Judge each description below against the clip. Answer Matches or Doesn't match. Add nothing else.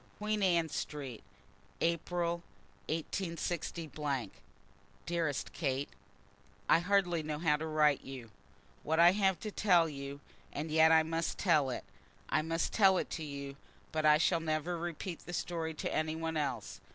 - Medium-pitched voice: Matches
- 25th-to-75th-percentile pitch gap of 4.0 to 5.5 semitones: Doesn't match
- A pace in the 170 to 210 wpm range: Doesn't match